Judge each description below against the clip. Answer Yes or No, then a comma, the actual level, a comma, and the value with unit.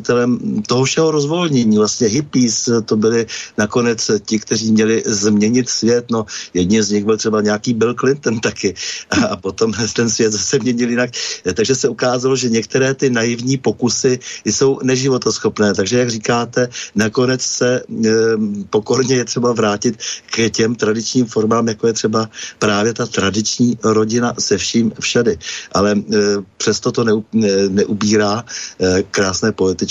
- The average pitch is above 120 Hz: No, low, 115 Hz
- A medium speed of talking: Yes, average, 140 wpm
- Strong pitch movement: No, narrow, 2.5 semitones